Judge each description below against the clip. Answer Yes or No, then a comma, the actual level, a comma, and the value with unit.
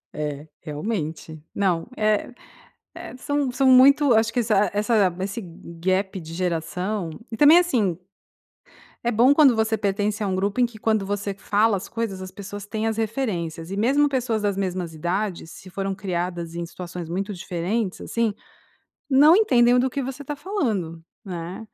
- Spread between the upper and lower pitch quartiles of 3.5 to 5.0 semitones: Yes, average, 4.7 semitones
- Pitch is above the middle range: Yes, high, 205 Hz